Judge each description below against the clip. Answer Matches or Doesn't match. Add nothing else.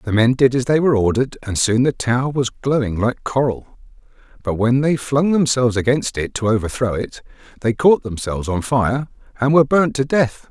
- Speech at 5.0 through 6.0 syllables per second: Matches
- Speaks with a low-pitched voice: Matches